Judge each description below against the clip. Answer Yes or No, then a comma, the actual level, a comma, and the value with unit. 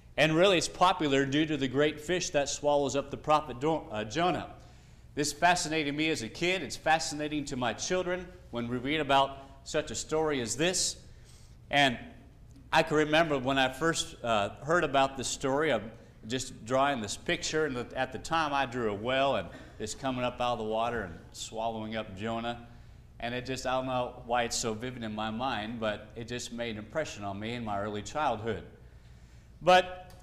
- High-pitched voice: No, low, 130 Hz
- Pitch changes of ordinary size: Yes, average, 4.9 semitones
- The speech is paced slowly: No, average, 200 wpm